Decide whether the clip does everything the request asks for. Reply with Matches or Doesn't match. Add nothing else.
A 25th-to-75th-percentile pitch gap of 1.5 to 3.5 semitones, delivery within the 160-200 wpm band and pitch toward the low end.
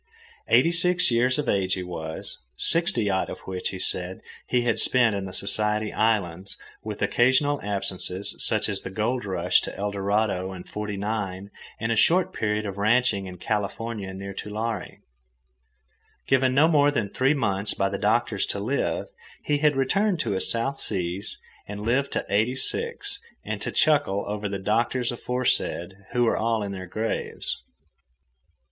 Doesn't match